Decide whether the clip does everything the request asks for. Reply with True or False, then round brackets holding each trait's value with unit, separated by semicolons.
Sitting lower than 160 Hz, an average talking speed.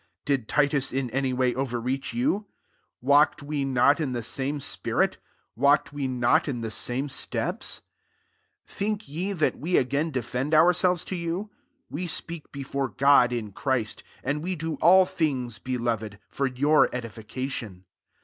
True (140 Hz; 150 wpm)